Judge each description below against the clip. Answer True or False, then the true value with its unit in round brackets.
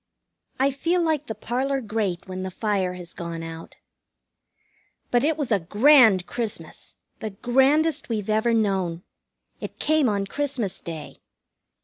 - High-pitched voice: True (220 Hz)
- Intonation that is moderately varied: False (6.5 semitones)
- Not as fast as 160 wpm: True (140 wpm)